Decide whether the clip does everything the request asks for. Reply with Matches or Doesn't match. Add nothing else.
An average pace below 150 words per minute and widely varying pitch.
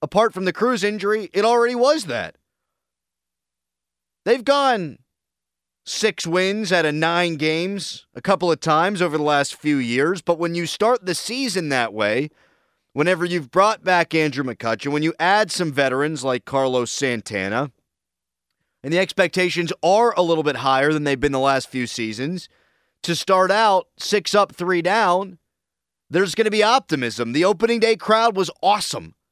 Doesn't match